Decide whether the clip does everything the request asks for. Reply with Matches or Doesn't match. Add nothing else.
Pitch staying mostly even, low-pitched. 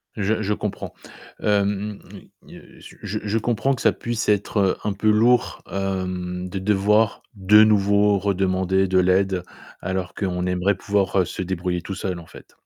Matches